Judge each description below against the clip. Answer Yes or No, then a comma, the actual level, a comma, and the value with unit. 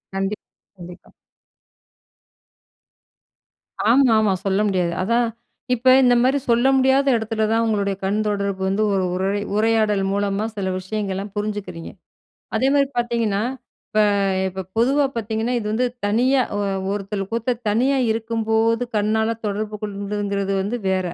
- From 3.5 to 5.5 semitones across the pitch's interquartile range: No, average, 2.7 semitones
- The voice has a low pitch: No, high, 215 Hz